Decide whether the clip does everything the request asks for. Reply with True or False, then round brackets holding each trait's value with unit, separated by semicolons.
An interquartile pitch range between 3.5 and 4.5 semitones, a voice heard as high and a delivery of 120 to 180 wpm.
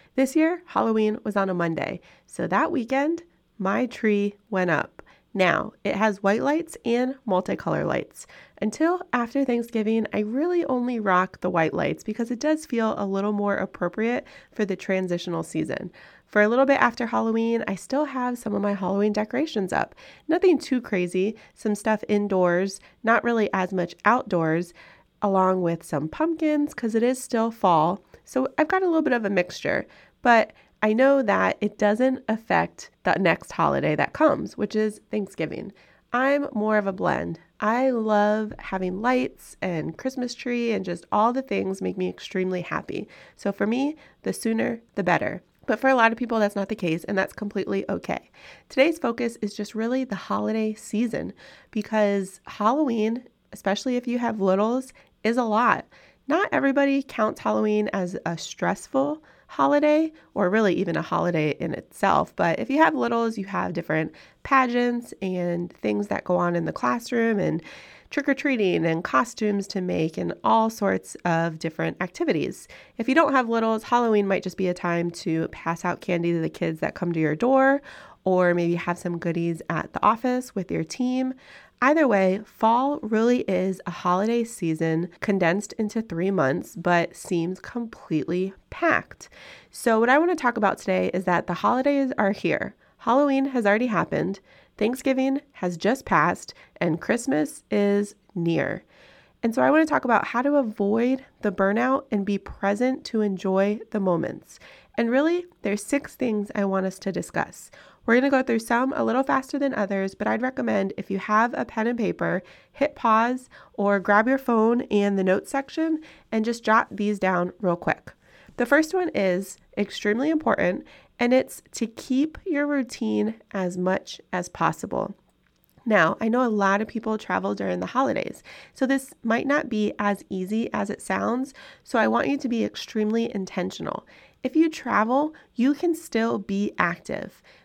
False (5.1 semitones; 215 Hz; 175 wpm)